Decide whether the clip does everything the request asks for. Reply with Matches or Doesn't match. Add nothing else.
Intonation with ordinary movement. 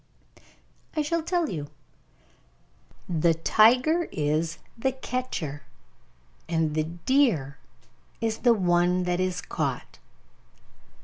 Doesn't match